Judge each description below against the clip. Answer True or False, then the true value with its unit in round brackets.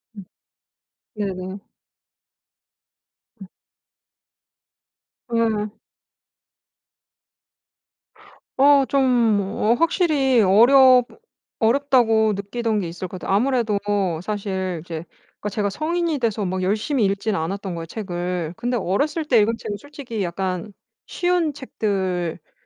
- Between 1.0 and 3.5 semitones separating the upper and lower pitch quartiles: False (5.3 semitones)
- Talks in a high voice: True (210 Hz)